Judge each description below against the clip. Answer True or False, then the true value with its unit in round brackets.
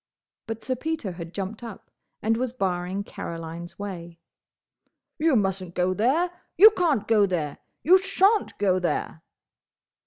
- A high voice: True (205 Hz)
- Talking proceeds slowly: True (125 wpm)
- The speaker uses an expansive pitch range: True (7.1 semitones)